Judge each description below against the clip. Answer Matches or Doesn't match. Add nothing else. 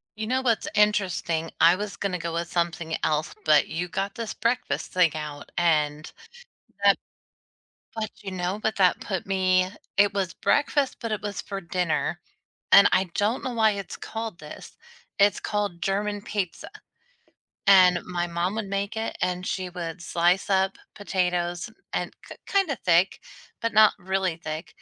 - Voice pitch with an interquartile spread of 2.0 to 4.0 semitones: Matches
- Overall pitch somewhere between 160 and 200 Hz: Matches